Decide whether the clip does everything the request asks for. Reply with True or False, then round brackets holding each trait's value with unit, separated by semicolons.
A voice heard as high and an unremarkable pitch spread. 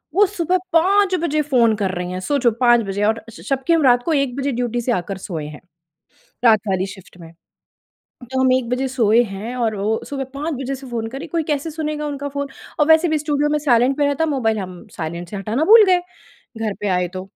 False (255 Hz; 5.9 semitones)